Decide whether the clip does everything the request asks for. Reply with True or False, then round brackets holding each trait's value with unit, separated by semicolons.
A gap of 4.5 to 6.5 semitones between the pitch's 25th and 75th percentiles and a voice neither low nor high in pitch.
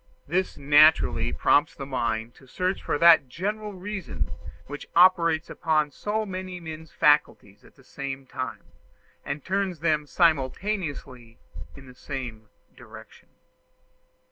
True (5.2 semitones; 155 Hz)